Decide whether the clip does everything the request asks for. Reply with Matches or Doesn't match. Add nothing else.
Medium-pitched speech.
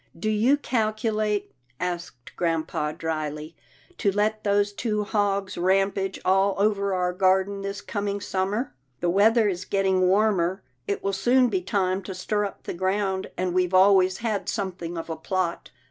Doesn't match